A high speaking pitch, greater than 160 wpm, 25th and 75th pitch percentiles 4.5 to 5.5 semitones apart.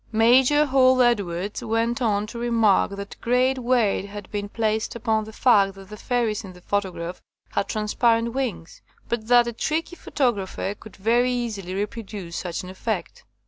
No: high, 220 Hz; average, 170 wpm; average, 3.3 semitones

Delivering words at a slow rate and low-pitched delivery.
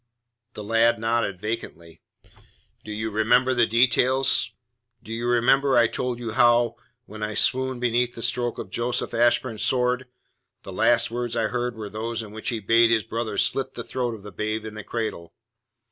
No: average, 180 wpm; low, 115 Hz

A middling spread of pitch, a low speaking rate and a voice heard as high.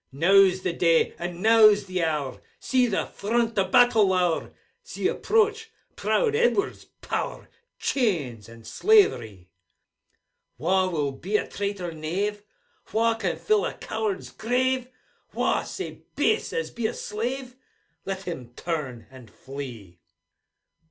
No: wide, 6.9 semitones; slow, 130 wpm; high, 195 Hz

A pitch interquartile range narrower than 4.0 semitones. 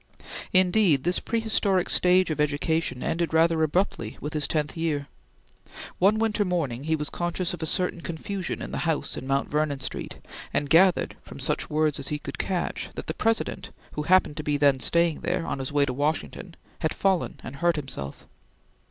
Yes: average, 3.6 semitones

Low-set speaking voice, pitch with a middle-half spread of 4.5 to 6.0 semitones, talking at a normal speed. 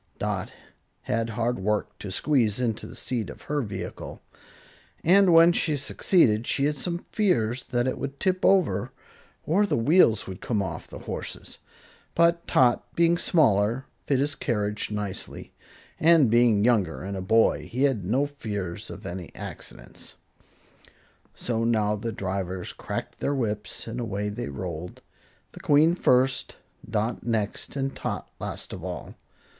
Yes: low, 115 Hz; wide, 5.6 semitones; average, 150 wpm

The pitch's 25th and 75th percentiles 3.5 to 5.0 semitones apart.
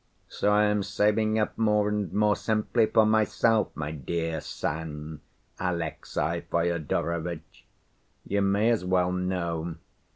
Yes: average, 4.3 semitones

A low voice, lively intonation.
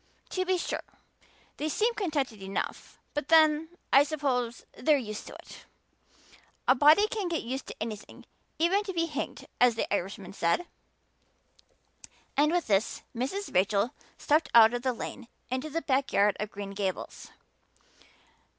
No: very high, 270 Hz; wide, 6.7 semitones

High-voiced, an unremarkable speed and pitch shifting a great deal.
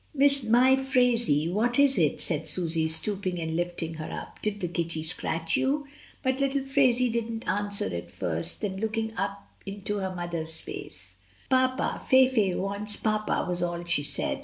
Yes: high, 200 Hz; average, 165 wpm; wide, 6.7 semitones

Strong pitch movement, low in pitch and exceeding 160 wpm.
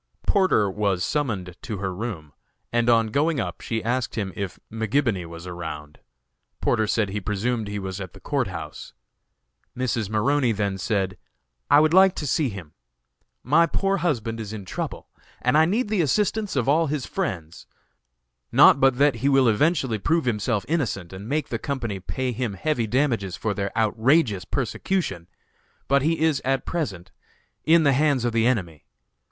Yes: wide, 6.4 semitones; low, 115 Hz; average, 170 wpm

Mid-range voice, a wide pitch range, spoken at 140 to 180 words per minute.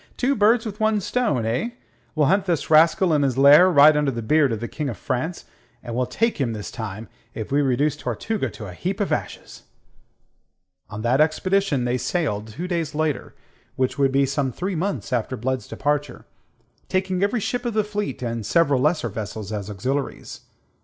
No: medium, 145 Hz; wide, 7.0 semitones; average, 190 wpm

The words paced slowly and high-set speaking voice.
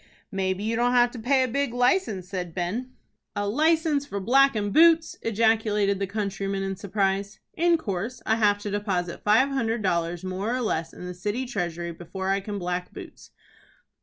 No: average, 180 wpm; high, 205 Hz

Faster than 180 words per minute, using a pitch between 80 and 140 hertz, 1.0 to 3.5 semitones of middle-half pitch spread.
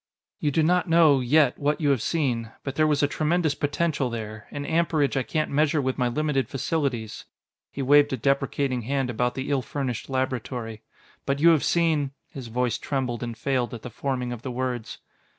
Yes: average, 200 wpm; low, 135 Hz; average, 3.2 semitones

